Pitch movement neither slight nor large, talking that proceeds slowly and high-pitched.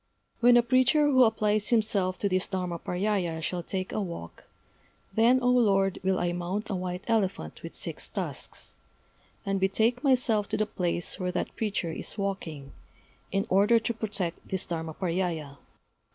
No: average, 3.8 semitones; average, 155 wpm; high, 195 Hz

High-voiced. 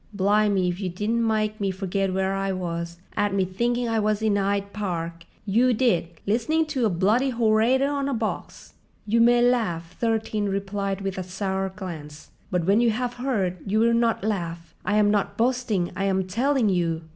Yes: high, 205 Hz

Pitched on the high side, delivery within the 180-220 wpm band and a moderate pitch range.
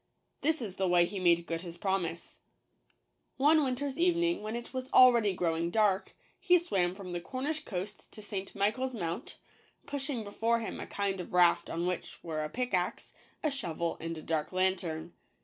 No: high, 195 Hz; average, 185 wpm; wide, 6.6 semitones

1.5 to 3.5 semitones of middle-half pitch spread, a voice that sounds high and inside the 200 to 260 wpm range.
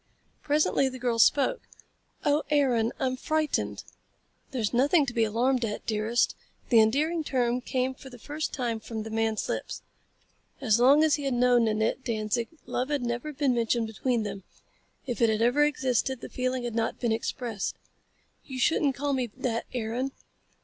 No: average, 3.1 semitones; high, 245 Hz; average, 170 wpm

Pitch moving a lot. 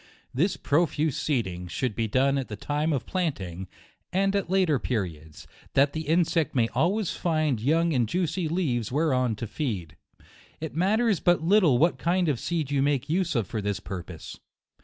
Yes: wide, 6.7 semitones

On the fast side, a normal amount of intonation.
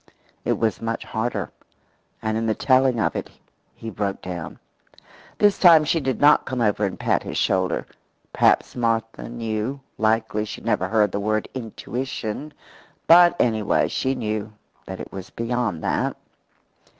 No: average, 155 wpm; average, 3.2 semitones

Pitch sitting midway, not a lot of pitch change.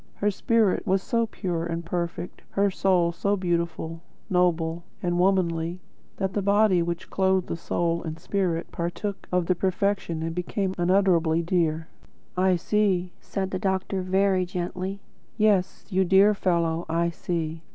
Yes: medium, 180 Hz; narrow, 2.3 semitones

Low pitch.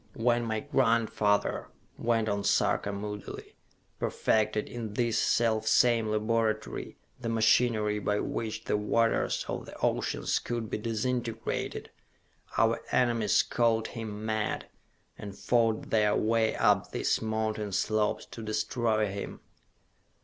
Yes: low, 110 Hz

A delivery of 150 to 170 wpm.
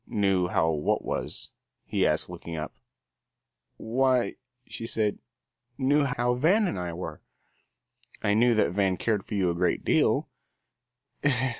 No: average, 140 wpm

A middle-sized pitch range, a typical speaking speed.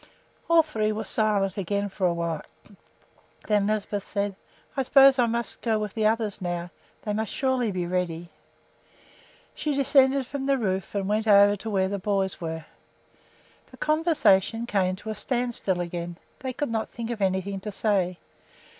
Yes: average, 3.8 semitones; average, 170 wpm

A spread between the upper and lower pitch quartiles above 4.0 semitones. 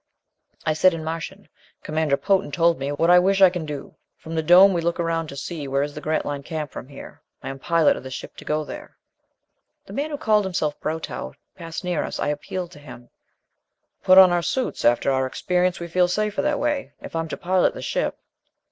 No: average, 3.7 semitones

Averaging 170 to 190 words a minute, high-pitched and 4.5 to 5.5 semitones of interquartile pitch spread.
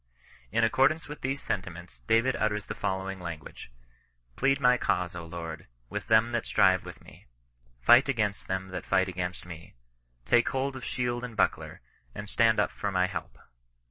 No: average, 175 wpm; low, 105 Hz; average, 5.1 semitones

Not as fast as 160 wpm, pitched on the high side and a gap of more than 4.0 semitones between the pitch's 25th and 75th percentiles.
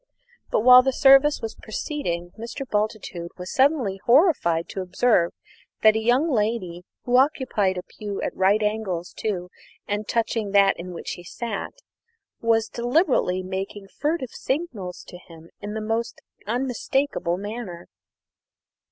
Yes: average, 140 wpm; high, 215 Hz; average, 5.0 semitones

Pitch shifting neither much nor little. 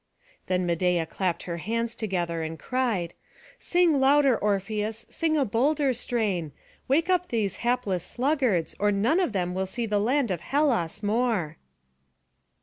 No: wide, 6.3 semitones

